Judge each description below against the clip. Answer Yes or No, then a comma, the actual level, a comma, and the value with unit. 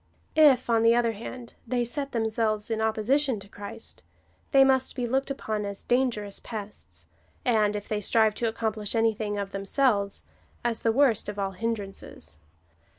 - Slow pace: No, average, 165 wpm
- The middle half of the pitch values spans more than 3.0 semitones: No, average, 2.7 semitones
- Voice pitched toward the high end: Yes, high, 225 Hz